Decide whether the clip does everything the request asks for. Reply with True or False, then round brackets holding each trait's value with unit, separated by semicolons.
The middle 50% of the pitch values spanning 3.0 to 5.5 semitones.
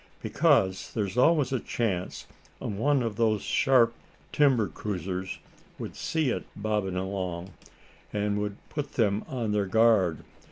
True (4.0 semitones)